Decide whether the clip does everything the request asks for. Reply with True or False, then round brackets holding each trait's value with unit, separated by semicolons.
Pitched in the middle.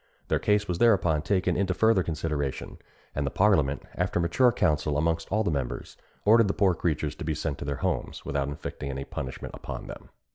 False (85 Hz)